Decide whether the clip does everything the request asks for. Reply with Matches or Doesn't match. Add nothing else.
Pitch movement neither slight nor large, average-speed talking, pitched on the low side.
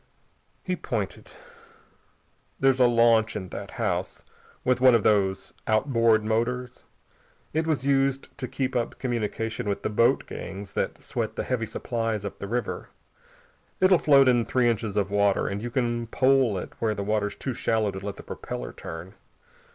Matches